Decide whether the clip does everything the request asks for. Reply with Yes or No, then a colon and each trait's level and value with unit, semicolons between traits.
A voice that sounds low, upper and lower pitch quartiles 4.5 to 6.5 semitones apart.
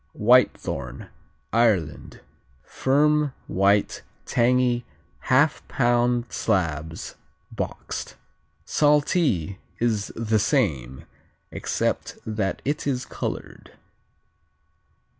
Yes: low, 115 Hz; average, 5.0 semitones